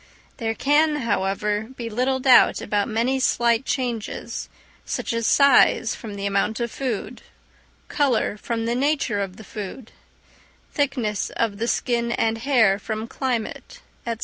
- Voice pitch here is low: No, high, 230 Hz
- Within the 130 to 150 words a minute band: Yes, average, 145 wpm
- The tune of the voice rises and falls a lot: No, average, 3.1 semitones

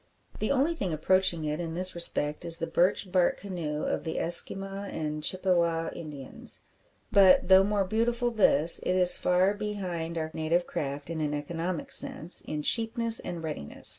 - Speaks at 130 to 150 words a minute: No, average, 170 wpm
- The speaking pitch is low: No, medium, 175 Hz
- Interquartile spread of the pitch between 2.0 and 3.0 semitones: No, average, 3.5 semitones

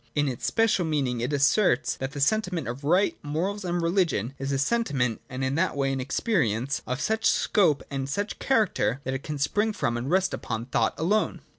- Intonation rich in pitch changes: Yes, wide, 6.2 semitones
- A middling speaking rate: No, fast, 225 wpm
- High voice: No, medium, 145 Hz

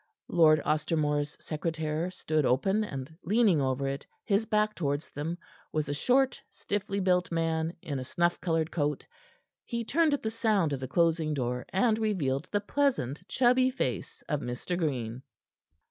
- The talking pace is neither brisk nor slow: Yes, average, 160 wpm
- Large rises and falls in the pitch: Yes, wide, 6.0 semitones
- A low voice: No, medium, 165 Hz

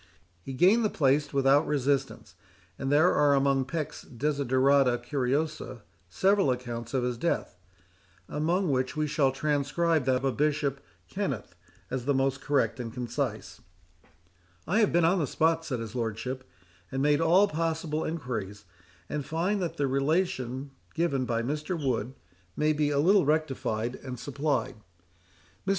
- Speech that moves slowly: No, average, 145 wpm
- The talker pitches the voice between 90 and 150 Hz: Yes, medium, 140 Hz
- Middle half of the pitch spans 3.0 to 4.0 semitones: Yes, average, 3.7 semitones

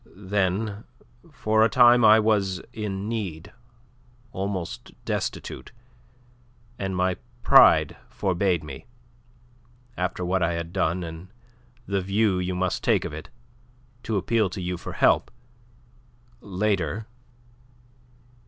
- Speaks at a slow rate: Yes, slow, 115 wpm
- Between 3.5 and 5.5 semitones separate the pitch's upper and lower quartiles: No, average, 2.9 semitones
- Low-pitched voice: Yes, very low, 95 Hz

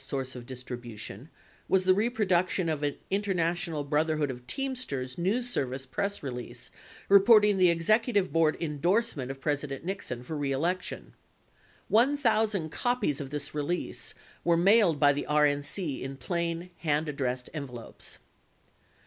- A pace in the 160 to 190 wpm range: No, average, 140 wpm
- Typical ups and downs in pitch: No, wide, 5.9 semitones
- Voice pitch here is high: No, medium, 160 Hz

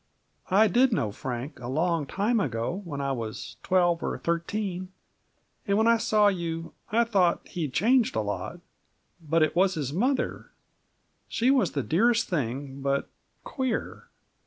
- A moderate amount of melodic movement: No, wide, 7.4 semitones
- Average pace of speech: Yes, average, 155 wpm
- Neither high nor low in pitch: Yes, medium, 175 Hz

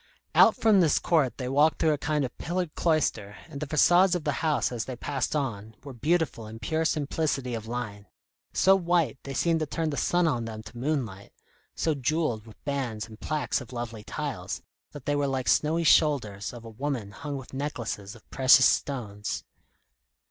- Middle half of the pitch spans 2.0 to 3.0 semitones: No, average, 5.1 semitones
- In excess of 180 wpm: Yes, average, 190 wpm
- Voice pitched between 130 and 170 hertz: Yes, medium, 140 Hz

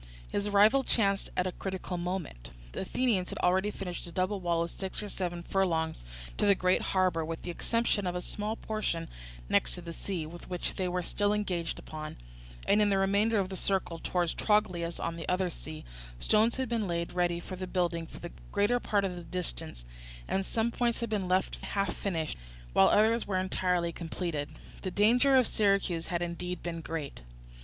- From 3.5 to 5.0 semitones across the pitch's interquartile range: No, average, 3.1 semitones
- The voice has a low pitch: No, medium, 185 Hz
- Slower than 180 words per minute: No, average, 190 wpm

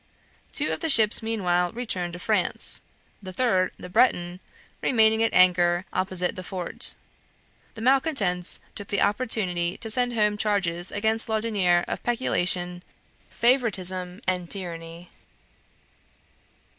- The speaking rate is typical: No, slow, 120 wpm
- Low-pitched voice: No, high, 190 Hz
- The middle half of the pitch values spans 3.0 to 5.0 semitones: Yes, average, 3.9 semitones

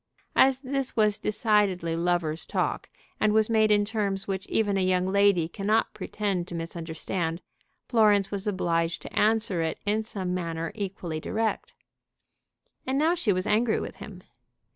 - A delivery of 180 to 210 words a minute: No, average, 155 wpm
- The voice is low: No, high, 200 Hz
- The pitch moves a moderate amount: Yes, average, 3.6 semitones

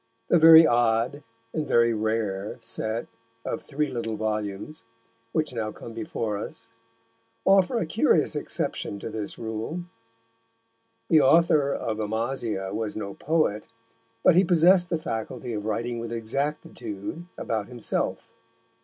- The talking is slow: Yes, slow, 130 wpm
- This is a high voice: No, low, 115 Hz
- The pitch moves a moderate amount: No, wide, 5.9 semitones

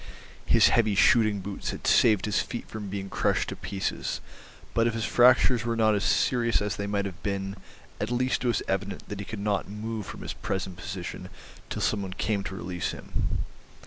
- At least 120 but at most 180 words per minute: No, fast, 205 wpm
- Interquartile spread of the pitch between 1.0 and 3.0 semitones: Yes, average, 2.7 semitones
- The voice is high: No, low, 105 Hz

